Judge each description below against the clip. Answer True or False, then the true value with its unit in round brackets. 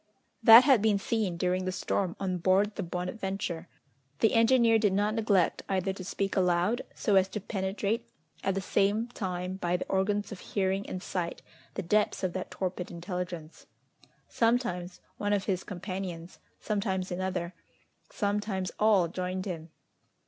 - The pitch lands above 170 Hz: True (190 Hz)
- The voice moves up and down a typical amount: False (2.3 semitones)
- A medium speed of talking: True (155 wpm)